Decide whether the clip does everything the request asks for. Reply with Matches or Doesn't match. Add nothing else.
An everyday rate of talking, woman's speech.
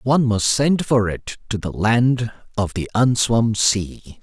Doesn't match